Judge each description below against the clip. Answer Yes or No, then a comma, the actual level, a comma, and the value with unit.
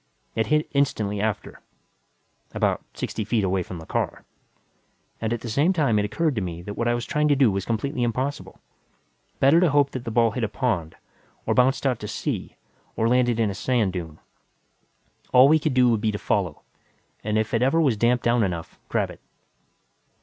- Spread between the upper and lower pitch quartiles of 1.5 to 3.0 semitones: No, average, 4.2 semitones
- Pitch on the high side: No, low, 120 Hz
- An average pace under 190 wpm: No, average, 200 wpm